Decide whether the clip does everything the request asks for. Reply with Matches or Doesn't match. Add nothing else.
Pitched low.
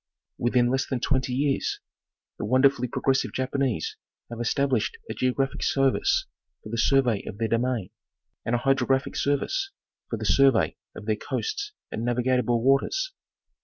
Matches